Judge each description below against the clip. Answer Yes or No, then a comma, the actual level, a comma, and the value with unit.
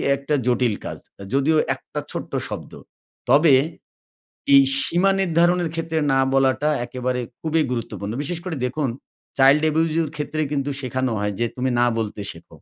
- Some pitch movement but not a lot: Yes, average, 4.1 semitones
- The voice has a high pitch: No, medium, 140 Hz